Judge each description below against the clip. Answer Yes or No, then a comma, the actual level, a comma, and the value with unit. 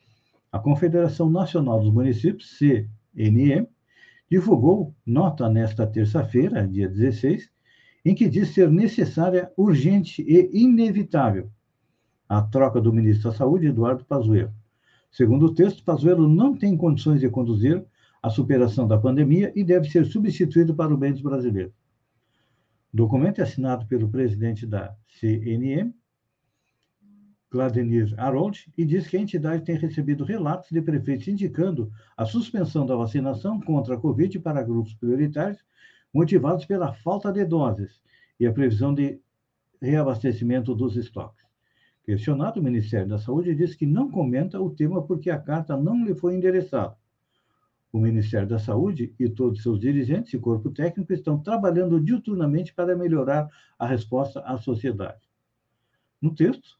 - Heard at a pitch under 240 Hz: Yes, medium, 140 Hz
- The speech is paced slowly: No, average, 140 wpm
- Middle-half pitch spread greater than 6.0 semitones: Yes, wide, 6.9 semitones